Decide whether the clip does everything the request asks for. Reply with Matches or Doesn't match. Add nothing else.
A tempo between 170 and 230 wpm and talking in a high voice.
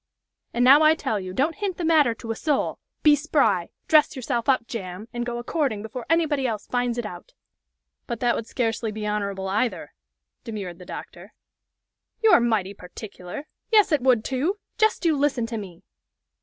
Matches